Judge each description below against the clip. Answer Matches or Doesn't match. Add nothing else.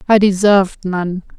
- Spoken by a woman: Matches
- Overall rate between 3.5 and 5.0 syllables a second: Matches